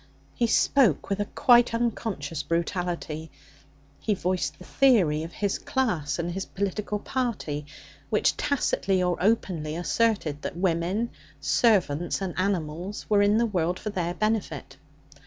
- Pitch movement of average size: Yes, average, 4.4 semitones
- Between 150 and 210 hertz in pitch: Yes, medium, 185 Hz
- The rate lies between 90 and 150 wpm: Yes, average, 140 wpm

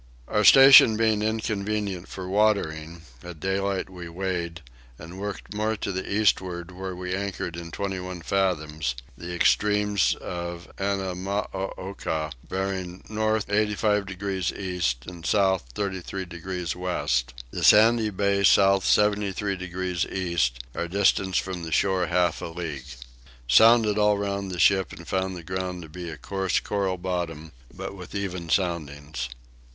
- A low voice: Yes, very low, 95 Hz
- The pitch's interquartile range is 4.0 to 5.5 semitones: No, narrow, 2.5 semitones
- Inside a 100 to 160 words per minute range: Yes, average, 145 wpm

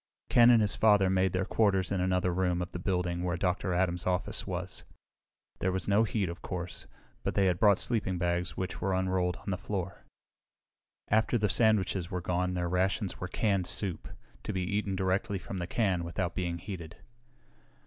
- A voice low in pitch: Yes, very low, 95 Hz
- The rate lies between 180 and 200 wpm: Yes, average, 190 wpm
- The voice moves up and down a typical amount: No, narrow, 1.9 semitones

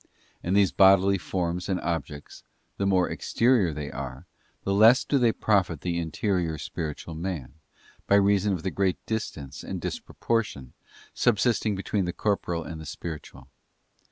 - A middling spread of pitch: Yes, average, 3.8 semitones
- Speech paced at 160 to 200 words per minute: No, average, 150 wpm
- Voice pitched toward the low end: Yes, very low, 95 Hz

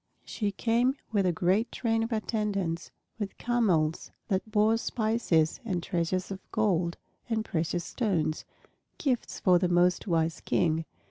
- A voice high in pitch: Yes, high, 195 Hz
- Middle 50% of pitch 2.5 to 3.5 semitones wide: No, average, 4.6 semitones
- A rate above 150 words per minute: No, average, 140 wpm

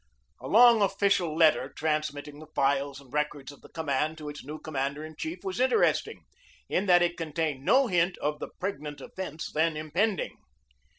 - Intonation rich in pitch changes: No, average, 3.8 semitones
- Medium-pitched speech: Yes, medium, 155 Hz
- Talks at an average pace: Yes, average, 175 wpm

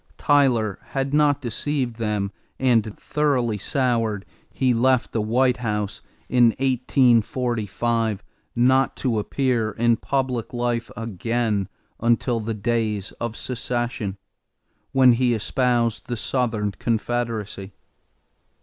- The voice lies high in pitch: No, low, 120 Hz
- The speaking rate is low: Yes, slow, 105 wpm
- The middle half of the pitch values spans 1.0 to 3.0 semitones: Yes, average, 2.7 semitones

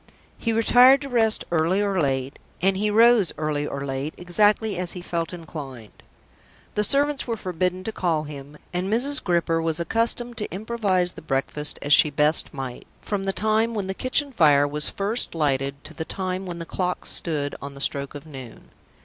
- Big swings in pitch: Yes, wide, 6.2 semitones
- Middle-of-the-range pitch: Yes, medium, 180 Hz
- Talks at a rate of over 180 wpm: Yes, average, 190 wpm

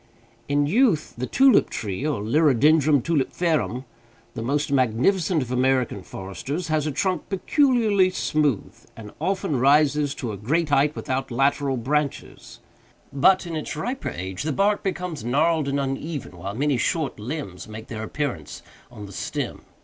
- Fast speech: No, average, 150 wpm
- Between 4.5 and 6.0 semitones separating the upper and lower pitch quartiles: Yes, average, 4.9 semitones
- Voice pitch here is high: No, medium, 145 Hz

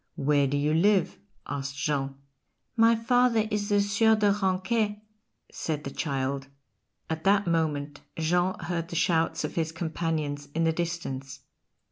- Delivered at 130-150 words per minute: Yes, average, 145 wpm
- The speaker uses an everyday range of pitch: No, wide, 5.9 semitones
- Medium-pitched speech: Yes, medium, 165 Hz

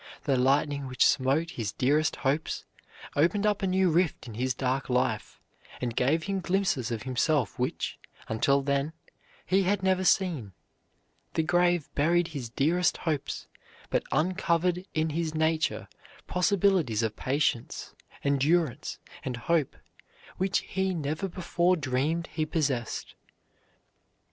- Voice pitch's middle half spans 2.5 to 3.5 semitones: No, average, 5.0 semitones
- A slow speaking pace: Yes, slow, 130 wpm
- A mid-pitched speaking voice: Yes, medium, 155 Hz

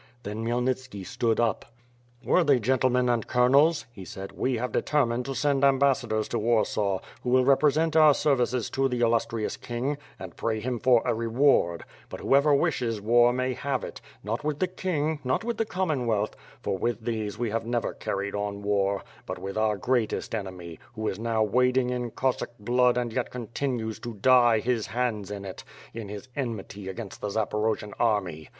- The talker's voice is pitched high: No, low, 120 Hz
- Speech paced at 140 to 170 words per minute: No, average, 185 wpm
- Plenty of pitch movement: No, average, 3.2 semitones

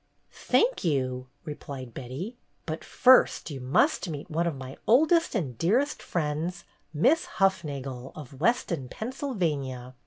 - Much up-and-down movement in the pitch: Yes, wide, 7.9 semitones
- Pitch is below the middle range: No, medium, 155 Hz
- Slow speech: Yes, slow, 130 wpm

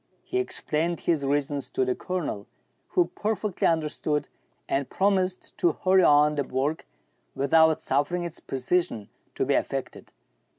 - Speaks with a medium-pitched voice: Yes, medium, 155 Hz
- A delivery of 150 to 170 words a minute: No, average, 140 wpm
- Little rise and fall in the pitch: No, average, 4.4 semitones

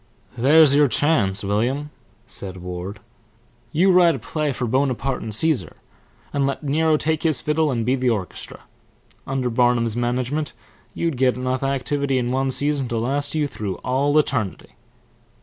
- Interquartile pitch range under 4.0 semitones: Yes, average, 3.6 semitones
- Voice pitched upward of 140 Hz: No, low, 130 Hz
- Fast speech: No, average, 155 wpm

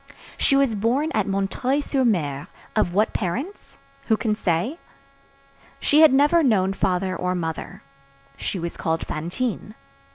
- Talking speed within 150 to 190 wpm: No, average, 140 wpm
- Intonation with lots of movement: Yes, wide, 6.8 semitones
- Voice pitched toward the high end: Yes, high, 210 Hz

